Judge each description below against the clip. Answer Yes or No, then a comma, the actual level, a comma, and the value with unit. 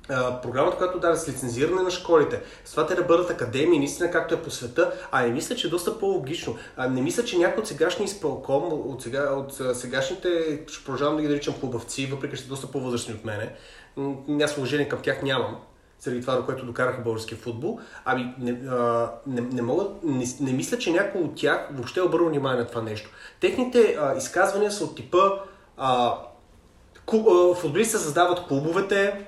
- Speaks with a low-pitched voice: No, medium, 145 Hz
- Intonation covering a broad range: Yes, wide, 6.0 semitones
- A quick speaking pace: Yes, fast, 195 wpm